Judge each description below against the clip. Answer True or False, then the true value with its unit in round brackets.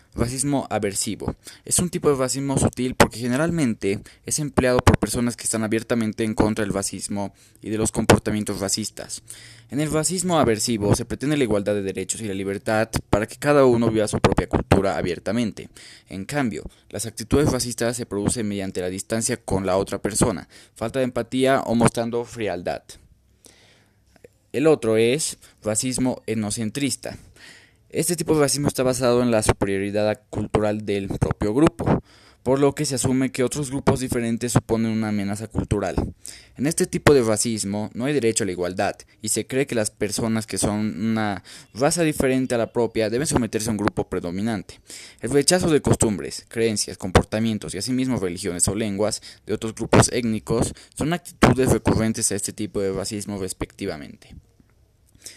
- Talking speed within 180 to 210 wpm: False (165 wpm)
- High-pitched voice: False (110 Hz)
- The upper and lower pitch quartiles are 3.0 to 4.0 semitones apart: True (3.7 semitones)